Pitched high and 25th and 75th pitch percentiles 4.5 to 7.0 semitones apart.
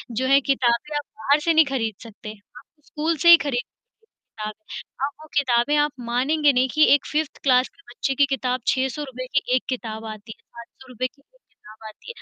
No: very high, 260 Hz; average, 3.8 semitones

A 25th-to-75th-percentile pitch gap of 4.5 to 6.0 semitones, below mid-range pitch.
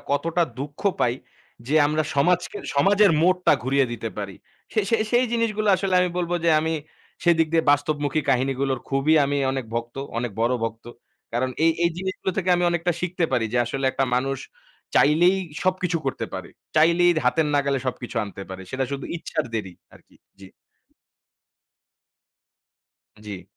No: average, 5.3 semitones; medium, 145 Hz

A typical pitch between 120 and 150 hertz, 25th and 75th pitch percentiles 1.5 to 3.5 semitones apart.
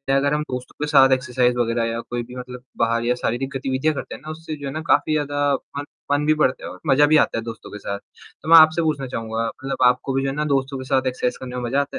Yes: low, 135 Hz; average, 2.7 semitones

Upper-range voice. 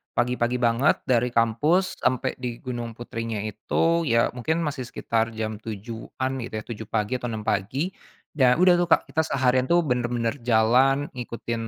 No: low, 120 Hz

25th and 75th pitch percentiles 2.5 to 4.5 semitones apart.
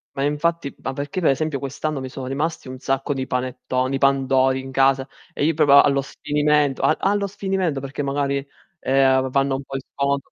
No: narrow, 1.8 semitones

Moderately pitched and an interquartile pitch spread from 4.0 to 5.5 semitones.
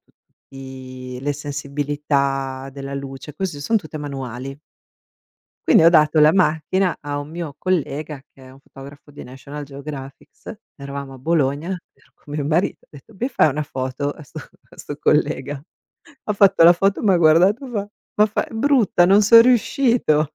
Yes: medium, 150 Hz; average, 4.4 semitones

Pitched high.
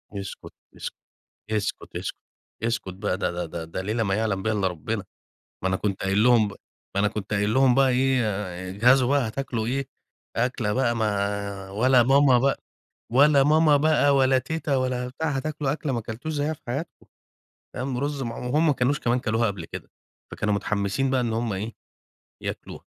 No: low, 120 Hz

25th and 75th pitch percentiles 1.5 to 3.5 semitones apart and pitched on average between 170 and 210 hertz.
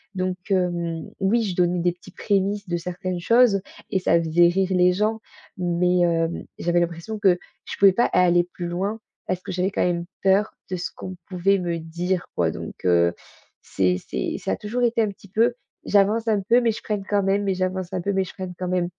Yes: narrow, 2.5 semitones; medium, 185 Hz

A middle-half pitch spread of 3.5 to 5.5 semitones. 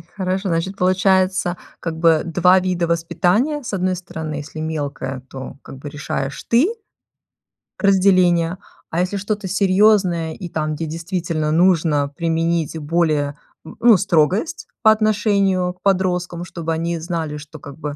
No: average, 2.9 semitones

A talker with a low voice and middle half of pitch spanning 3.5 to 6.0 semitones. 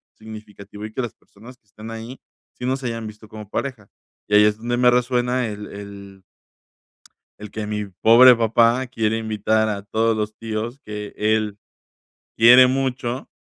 No: low, 110 Hz; narrow, 2.5 semitones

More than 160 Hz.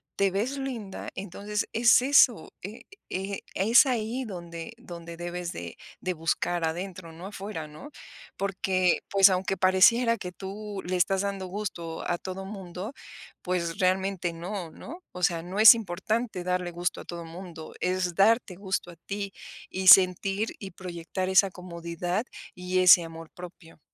Yes: medium, 185 Hz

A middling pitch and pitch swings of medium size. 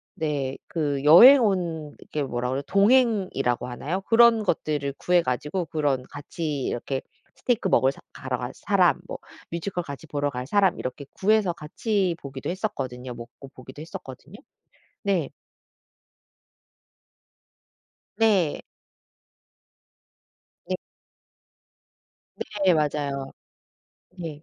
No: medium, 155 Hz; wide, 5.7 semitones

